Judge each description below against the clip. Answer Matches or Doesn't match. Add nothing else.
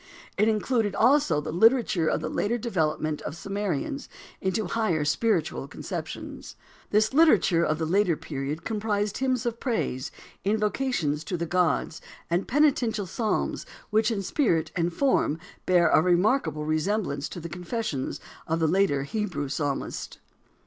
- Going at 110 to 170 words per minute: Matches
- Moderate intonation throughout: Doesn't match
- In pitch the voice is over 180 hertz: Matches